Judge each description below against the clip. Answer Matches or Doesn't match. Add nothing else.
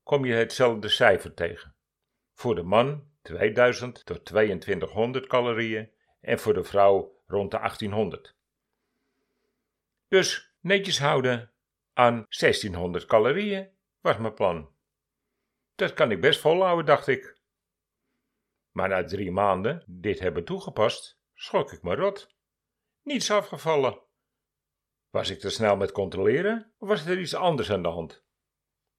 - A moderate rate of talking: Doesn't match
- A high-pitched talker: Doesn't match